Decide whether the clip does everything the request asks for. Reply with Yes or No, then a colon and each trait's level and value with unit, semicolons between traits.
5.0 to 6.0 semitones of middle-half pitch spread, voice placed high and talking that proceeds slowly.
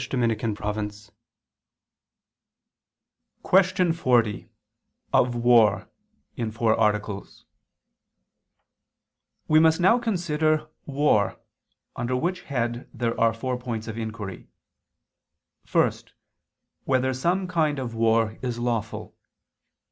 No: wide, 5.5 semitones; low, 120 Hz; slow, 90 wpm